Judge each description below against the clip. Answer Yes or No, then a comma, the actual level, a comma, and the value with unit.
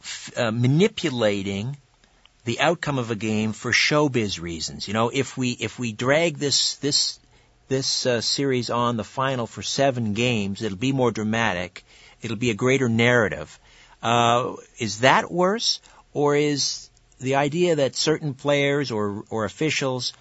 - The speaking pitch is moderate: No, low, 125 Hz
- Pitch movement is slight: No, average, 3.9 semitones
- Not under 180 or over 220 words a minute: No, average, 155 wpm